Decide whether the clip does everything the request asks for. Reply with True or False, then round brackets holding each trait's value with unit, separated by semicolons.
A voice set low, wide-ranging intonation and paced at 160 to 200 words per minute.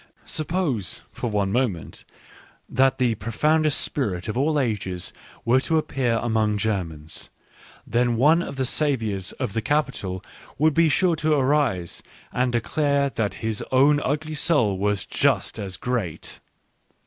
False (125 Hz; 6.0 semitones; 140 wpm)